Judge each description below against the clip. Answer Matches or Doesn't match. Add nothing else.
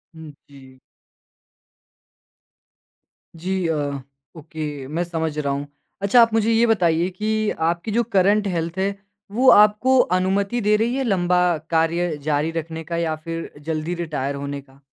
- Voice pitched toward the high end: Doesn't match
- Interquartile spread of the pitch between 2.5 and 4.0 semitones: Doesn't match